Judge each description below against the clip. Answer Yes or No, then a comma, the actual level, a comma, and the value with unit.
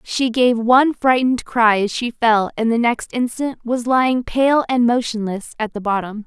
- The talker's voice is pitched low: No, high, 235 Hz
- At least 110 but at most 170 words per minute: No, average, 190 wpm